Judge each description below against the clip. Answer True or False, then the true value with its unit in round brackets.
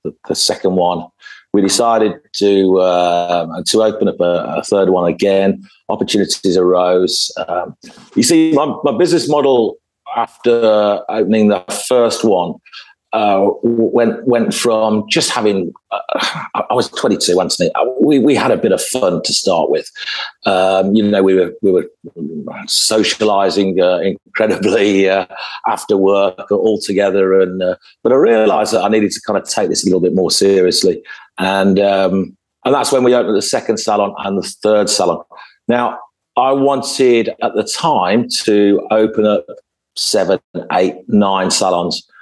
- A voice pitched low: True (105 Hz)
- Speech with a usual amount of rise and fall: True (4.0 semitones)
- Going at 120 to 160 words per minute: True (155 wpm)